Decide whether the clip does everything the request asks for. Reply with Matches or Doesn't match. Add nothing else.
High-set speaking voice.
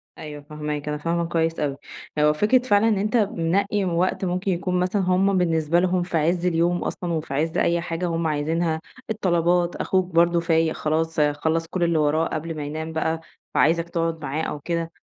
Doesn't match